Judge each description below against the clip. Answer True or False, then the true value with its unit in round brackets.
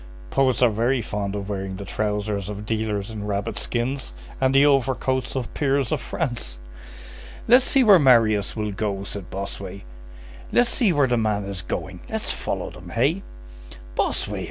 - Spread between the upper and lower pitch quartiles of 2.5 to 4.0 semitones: False (4.7 semitones)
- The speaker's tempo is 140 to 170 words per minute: True (165 wpm)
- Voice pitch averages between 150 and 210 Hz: False (110 Hz)